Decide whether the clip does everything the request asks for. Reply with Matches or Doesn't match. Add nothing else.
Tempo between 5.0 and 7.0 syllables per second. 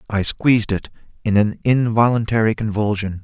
Matches